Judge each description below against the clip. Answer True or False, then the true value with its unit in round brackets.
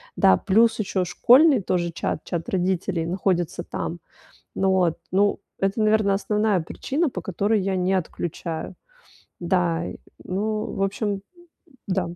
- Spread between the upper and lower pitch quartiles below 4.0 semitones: True (3.0 semitones)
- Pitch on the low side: False (190 Hz)